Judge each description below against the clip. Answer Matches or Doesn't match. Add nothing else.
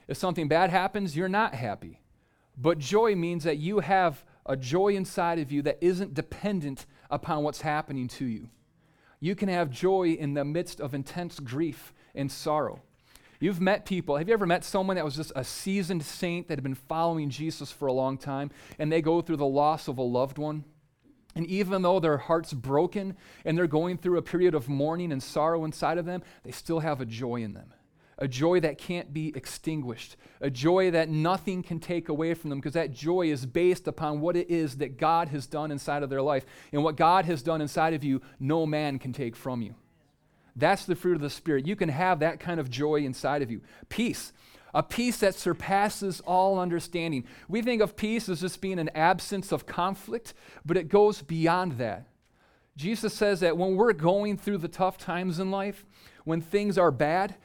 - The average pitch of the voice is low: Doesn't match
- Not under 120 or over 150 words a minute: Doesn't match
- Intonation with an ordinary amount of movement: Matches